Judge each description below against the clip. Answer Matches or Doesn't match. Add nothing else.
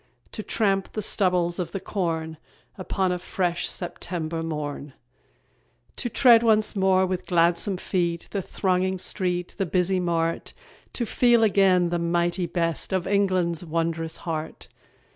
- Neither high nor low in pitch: Matches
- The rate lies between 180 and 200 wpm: Doesn't match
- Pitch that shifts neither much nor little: Doesn't match